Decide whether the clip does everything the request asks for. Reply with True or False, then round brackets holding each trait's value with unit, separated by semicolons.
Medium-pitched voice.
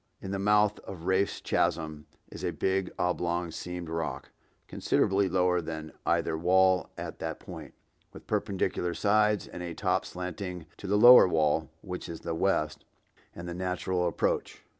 False (90 Hz)